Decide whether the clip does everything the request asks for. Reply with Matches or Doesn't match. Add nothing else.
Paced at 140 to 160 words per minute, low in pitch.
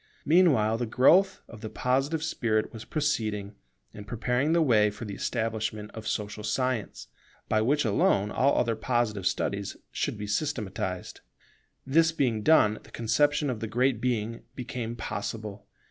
Matches